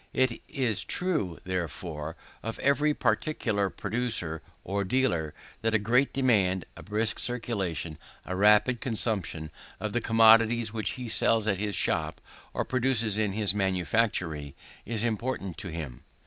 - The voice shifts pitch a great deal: No, average, 4.2 semitones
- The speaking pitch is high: No, low, 105 Hz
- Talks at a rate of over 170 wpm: No, average, 140 wpm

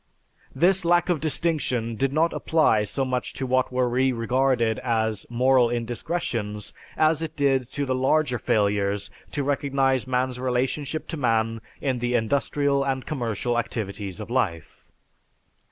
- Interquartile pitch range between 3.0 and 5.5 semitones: Yes, average, 3.5 semitones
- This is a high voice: No, low, 130 Hz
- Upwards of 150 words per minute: No, average, 145 wpm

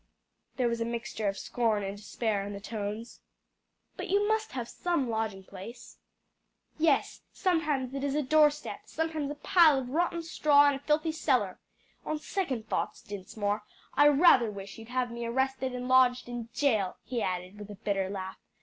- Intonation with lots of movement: Yes, wide, 5.8 semitones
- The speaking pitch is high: Yes, high, 245 Hz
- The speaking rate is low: No, average, 180 wpm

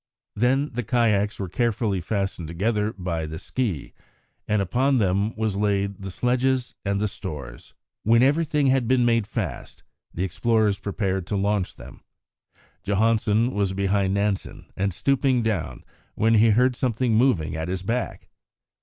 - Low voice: Yes, low, 105 Hz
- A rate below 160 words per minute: Yes, average, 150 wpm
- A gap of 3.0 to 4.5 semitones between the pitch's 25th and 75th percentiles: Yes, average, 3.7 semitones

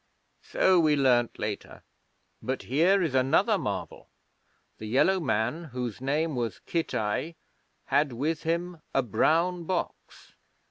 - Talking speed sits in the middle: No, slow, 125 wpm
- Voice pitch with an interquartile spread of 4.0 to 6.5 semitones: Yes, average, 5.1 semitones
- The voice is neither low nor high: Yes, medium, 145 Hz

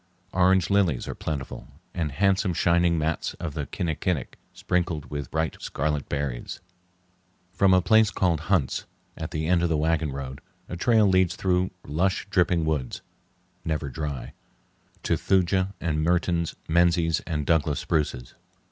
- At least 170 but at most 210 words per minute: No, average, 145 wpm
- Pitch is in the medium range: No, very low, 85 Hz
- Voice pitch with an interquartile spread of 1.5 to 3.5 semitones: Yes, average, 3.2 semitones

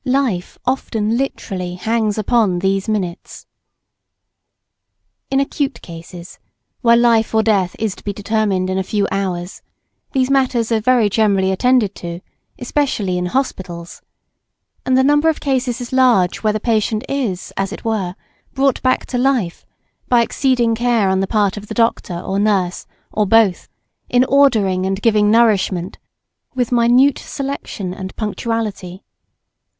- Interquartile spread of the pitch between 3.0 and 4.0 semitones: No, average, 4.5 semitones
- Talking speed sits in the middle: Yes, average, 145 wpm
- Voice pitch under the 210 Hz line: No, high, 220 Hz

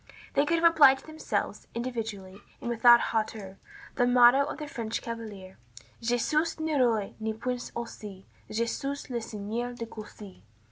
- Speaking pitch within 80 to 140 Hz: No, high, 235 Hz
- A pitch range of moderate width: Yes, average, 3.6 semitones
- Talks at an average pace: Yes, average, 160 wpm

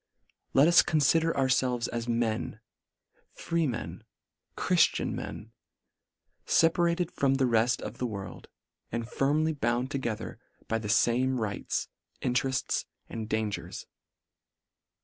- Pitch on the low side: Yes, low, 125 Hz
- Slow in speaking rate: Yes, slow, 120 wpm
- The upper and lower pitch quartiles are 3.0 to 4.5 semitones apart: Yes, average, 3.7 semitones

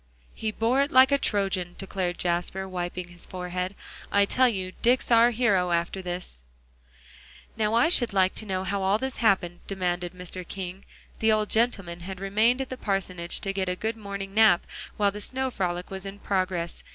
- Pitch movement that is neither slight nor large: Yes, average, 3.4 semitones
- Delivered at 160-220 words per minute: Yes, average, 190 wpm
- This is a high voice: Yes, high, 195 Hz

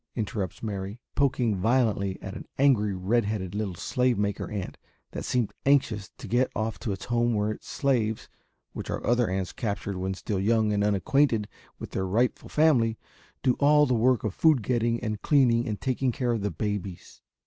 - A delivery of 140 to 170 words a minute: No, average, 185 wpm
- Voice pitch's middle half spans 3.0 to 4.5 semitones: Yes, average, 3.6 semitones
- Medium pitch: No, low, 110 Hz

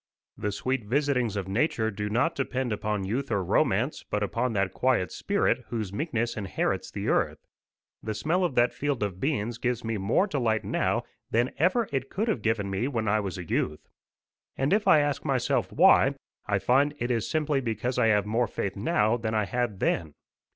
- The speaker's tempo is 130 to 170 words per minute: No, average, 195 wpm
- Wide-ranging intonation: No, average, 4.6 semitones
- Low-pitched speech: Yes, low, 115 Hz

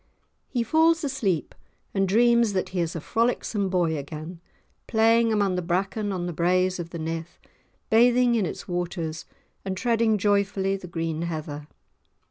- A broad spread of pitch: No, average, 4.8 semitones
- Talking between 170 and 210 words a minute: No, average, 155 wpm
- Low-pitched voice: No, high, 190 Hz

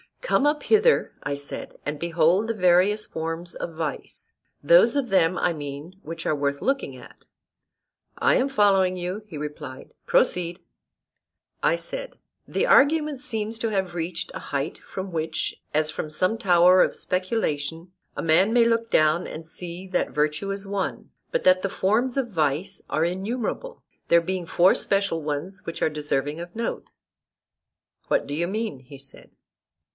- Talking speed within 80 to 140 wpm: No, average, 165 wpm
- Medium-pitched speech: Yes, medium, 180 Hz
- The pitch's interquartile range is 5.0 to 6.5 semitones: Yes, wide, 5.6 semitones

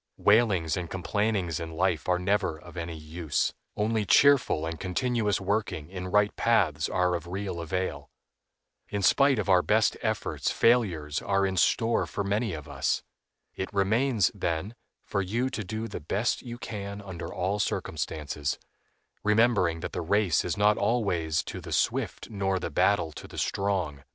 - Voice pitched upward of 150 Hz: No, very low, 95 Hz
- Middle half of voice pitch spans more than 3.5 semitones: Yes, average, 3.9 semitones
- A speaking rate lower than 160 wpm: No, average, 165 wpm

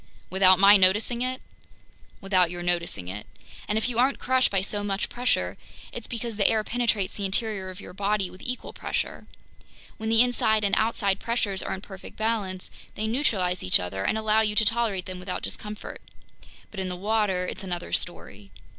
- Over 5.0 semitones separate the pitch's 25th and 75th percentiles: No, average, 3.1 semitones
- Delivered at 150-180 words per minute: No, average, 190 wpm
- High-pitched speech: Yes, high, 205 Hz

